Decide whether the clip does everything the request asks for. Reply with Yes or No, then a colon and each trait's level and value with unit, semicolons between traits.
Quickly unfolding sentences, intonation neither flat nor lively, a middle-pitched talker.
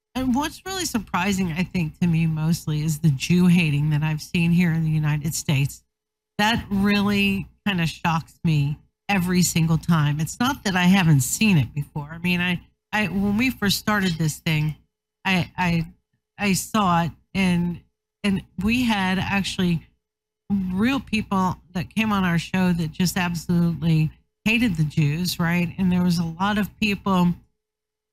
No: average, 170 wpm; average, 3.8 semitones; medium, 180 Hz